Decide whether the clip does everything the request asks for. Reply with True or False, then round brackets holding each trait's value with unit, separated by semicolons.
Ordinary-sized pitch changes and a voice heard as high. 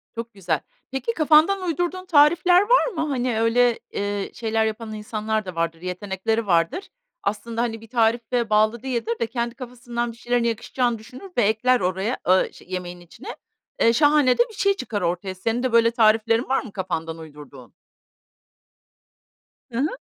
True (3.9 semitones; 230 Hz)